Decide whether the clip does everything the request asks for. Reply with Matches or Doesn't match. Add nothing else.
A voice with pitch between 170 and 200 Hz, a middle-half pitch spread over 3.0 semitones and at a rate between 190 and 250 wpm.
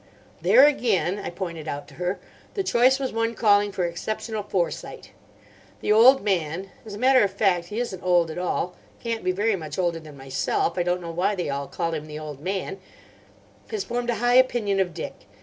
Matches